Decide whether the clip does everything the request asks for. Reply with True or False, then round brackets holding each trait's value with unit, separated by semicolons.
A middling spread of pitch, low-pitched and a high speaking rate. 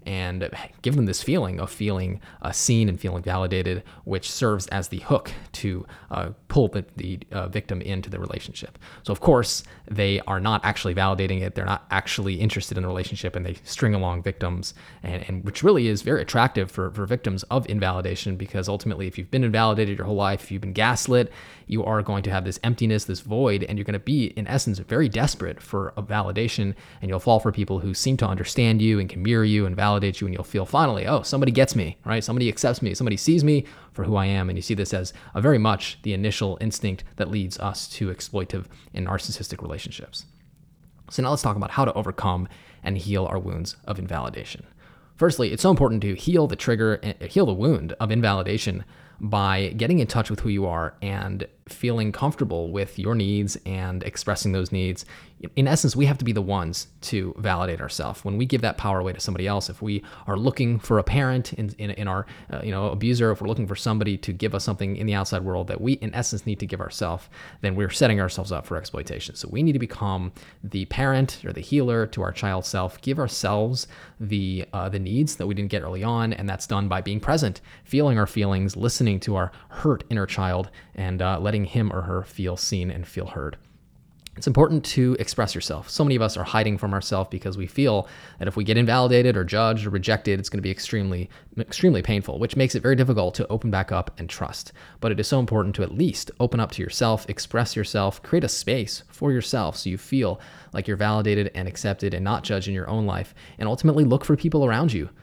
True (3.3 semitones; 100 Hz; 225 wpm)